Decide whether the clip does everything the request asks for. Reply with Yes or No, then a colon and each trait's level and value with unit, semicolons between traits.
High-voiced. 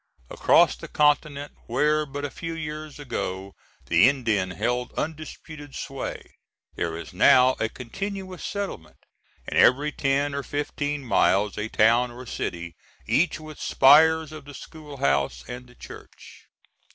No: medium, 140 Hz